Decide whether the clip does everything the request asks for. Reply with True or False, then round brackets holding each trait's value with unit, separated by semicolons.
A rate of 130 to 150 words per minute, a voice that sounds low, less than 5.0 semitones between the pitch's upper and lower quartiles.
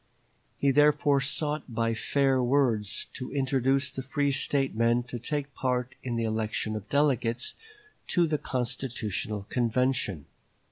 True (135 wpm; 130 Hz; 3.4 semitones)